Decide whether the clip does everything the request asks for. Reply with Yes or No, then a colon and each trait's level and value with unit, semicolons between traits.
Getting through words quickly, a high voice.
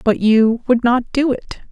Yes: fast, 210 wpm; high, 240 Hz